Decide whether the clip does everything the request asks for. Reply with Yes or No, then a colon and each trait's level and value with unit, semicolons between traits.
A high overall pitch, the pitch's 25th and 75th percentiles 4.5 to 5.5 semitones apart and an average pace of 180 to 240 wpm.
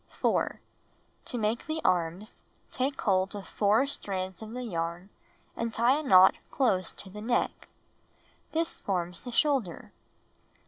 No: high, 210 Hz; average, 5.0 semitones; average, 140 wpm